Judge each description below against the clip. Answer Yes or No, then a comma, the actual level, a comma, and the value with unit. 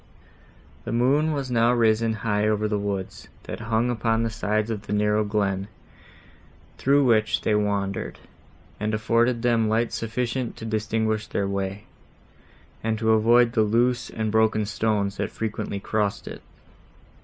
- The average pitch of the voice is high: No, low, 110 Hz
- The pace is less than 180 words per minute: Yes, average, 150 wpm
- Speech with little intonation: Yes, narrow, 1.7 semitones